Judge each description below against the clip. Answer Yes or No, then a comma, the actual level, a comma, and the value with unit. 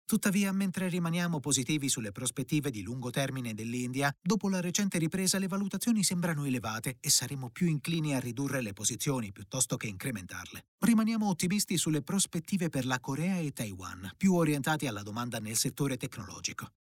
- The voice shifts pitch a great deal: Yes, wide, 6.4 semitones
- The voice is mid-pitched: Yes, medium, 145 Hz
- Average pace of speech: Yes, average, 160 wpm